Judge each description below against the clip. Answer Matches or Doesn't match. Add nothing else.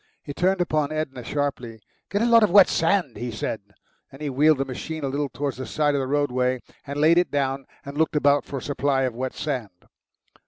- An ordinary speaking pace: Doesn't match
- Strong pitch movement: Doesn't match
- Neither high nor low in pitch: Matches